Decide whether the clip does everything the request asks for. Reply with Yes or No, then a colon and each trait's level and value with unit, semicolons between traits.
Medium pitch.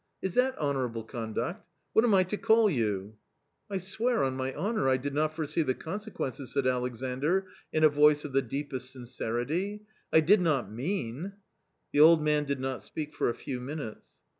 Yes: medium, 145 Hz